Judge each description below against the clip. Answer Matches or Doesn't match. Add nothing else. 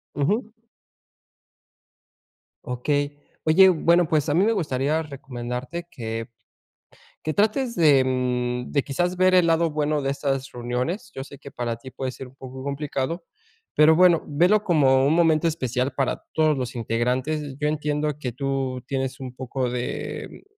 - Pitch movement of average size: Matches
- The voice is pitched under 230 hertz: Matches